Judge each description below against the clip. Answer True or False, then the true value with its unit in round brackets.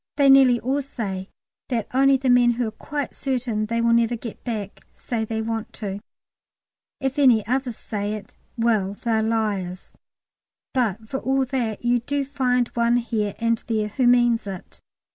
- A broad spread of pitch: False (2.7 semitones)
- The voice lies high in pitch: True (235 Hz)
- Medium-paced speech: True (170 wpm)